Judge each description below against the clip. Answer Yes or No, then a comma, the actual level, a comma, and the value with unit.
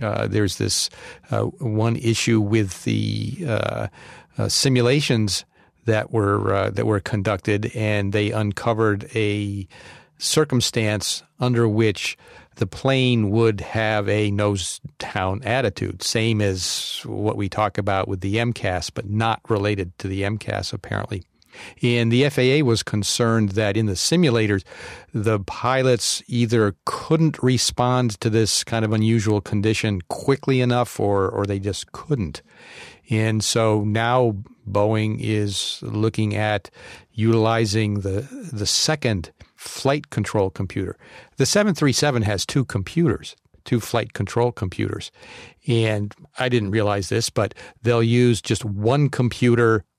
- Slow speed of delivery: Yes, slow, 130 wpm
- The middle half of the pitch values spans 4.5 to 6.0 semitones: No, narrow, 2.6 semitones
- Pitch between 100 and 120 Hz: Yes, low, 110 Hz